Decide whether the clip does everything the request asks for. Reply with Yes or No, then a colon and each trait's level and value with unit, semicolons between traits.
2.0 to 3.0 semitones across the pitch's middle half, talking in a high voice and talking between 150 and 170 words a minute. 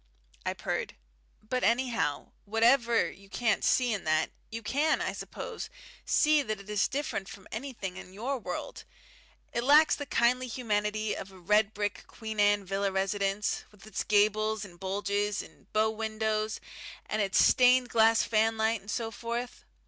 Yes: average, 2.7 semitones; high, 215 Hz; average, 160 wpm